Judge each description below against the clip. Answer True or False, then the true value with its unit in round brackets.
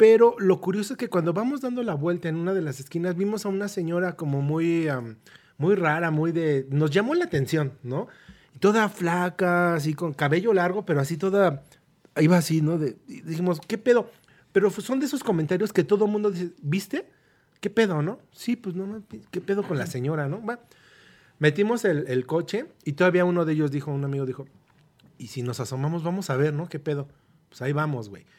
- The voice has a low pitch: False (170 Hz)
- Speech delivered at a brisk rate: True (210 wpm)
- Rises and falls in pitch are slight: False (5.0 semitones)